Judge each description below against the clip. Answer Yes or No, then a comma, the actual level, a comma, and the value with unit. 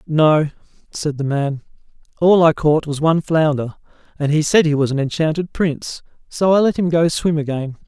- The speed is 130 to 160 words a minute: No, average, 190 wpm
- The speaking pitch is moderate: Yes, medium, 155 Hz